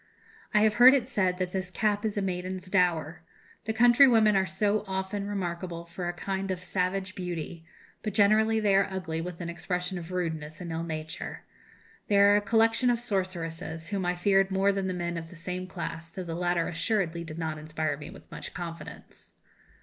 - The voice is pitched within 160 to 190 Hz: Yes, medium, 185 Hz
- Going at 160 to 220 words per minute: Yes, average, 195 wpm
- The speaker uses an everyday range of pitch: Yes, average, 3.1 semitones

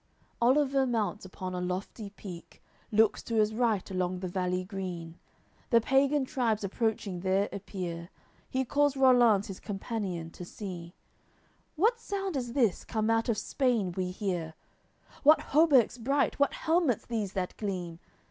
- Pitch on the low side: No, high, 210 Hz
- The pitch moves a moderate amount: No, wide, 5.7 semitones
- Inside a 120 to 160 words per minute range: Yes, average, 155 wpm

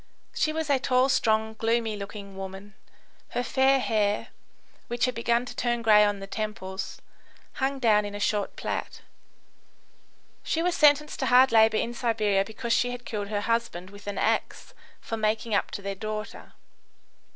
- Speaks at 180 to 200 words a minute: No, average, 170 wpm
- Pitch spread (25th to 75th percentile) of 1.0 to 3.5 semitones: Yes, average, 3.2 semitones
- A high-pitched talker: Yes, high, 220 Hz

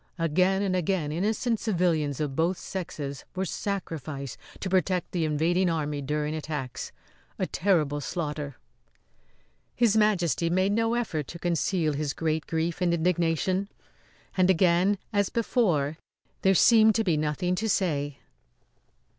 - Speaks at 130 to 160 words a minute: Yes, slow, 135 wpm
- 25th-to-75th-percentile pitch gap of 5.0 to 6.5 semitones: No, average, 4.0 semitones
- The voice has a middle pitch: Yes, medium, 170 Hz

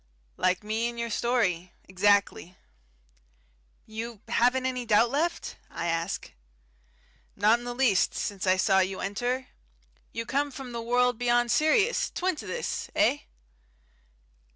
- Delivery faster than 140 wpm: No, slow, 135 wpm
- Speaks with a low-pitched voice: No, high, 235 Hz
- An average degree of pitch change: Yes, average, 4.0 semitones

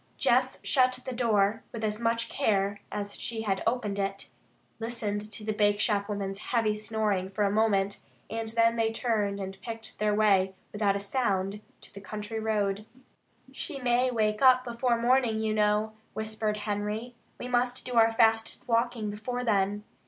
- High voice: Yes, high, 215 Hz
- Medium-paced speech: Yes, average, 165 wpm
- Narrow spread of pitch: Yes, narrow, 2.1 semitones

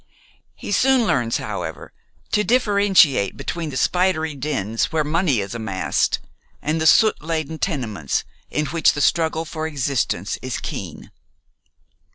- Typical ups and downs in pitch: No, wide, 6.1 semitones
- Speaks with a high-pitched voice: No, medium, 155 Hz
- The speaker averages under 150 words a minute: Yes, slow, 135 wpm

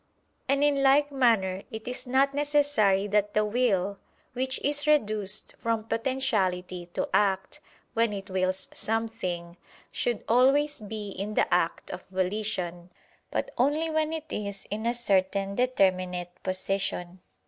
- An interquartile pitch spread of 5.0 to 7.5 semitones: Yes, wide, 5.5 semitones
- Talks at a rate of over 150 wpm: No, average, 140 wpm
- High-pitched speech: Yes, high, 215 Hz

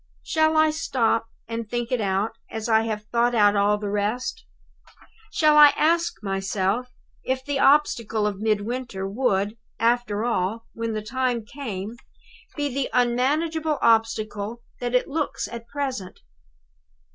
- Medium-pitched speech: No, high, 230 Hz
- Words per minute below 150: Yes, average, 140 wpm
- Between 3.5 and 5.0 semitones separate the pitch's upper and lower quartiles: Yes, average, 3.8 semitones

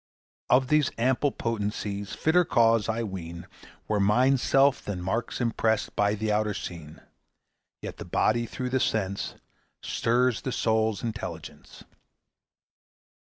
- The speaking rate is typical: No, slow, 125 wpm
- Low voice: Yes, low, 110 Hz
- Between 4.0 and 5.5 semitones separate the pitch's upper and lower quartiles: No, average, 3.5 semitones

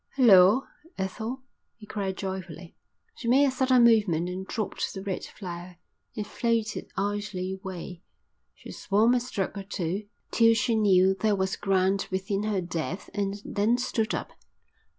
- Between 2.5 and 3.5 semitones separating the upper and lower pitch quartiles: Yes, average, 2.9 semitones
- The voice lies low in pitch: No, high, 200 Hz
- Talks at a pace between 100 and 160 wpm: Yes, average, 150 wpm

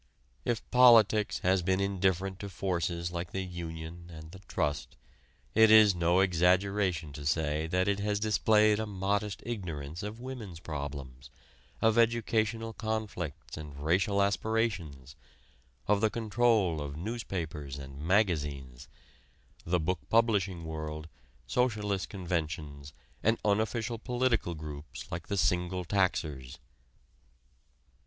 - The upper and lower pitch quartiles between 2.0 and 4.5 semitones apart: No, average, 5.1 semitones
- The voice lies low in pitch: Yes, very low, 95 Hz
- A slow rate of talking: Yes, slow, 120 wpm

